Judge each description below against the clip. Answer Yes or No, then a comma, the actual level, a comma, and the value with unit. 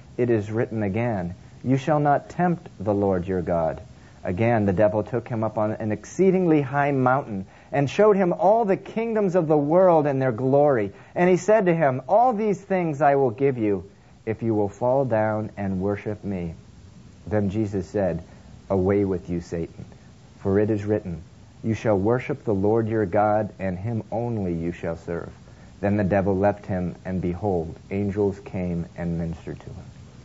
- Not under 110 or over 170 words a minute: No, average, 185 wpm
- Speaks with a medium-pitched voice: No, low, 110 Hz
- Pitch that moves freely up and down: Yes, wide, 5.8 semitones